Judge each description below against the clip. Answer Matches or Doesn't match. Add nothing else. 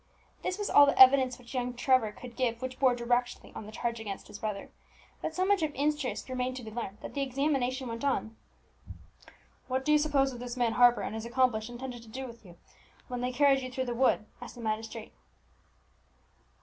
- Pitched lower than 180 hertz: Doesn't match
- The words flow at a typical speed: Doesn't match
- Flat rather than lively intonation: Matches